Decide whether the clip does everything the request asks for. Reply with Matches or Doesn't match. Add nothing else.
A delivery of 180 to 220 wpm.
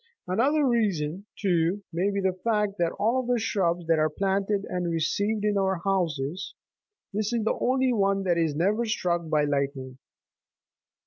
Doesn't match